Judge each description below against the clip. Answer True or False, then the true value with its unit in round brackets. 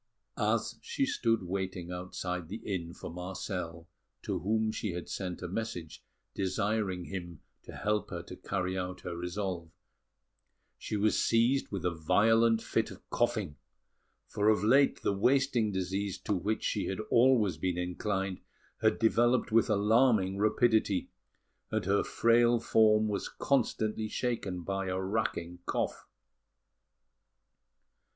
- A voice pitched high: False (100 Hz)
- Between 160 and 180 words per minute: False (135 wpm)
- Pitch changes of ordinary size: True (3.6 semitones)